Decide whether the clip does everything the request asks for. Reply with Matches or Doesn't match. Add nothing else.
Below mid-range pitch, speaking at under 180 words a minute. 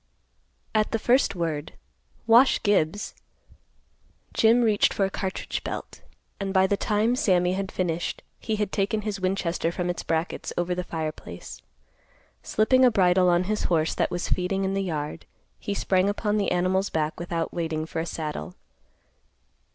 Doesn't match